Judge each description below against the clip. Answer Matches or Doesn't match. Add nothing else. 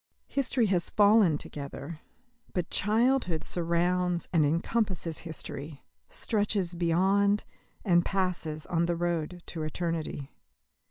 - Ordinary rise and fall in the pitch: Matches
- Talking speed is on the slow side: Matches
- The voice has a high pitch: Doesn't match